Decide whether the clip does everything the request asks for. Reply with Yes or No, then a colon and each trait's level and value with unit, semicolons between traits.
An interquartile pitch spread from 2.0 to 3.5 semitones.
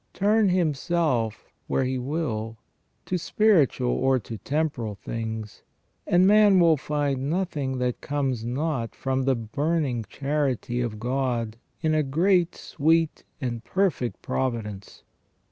No: wide, 5.4 semitones